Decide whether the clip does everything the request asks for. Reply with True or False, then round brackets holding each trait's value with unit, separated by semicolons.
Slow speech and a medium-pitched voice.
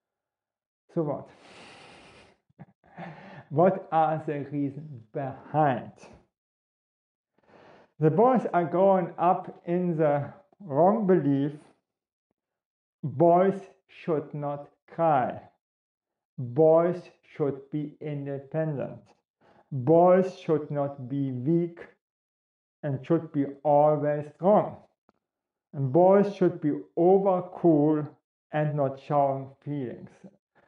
True (85 wpm; 155 Hz)